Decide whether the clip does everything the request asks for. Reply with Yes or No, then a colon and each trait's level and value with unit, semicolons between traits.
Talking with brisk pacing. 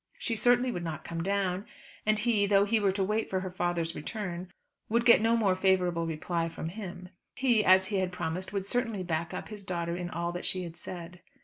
Yes: fast, 220 wpm